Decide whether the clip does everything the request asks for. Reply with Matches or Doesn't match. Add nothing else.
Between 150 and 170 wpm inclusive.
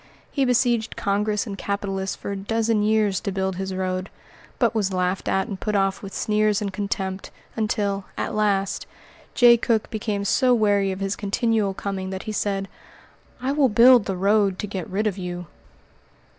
Doesn't match